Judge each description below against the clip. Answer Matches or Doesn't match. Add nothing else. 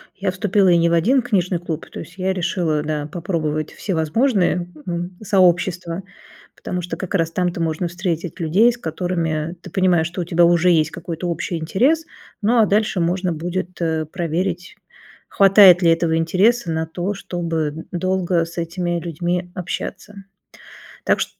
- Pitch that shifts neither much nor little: Doesn't match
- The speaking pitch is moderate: Matches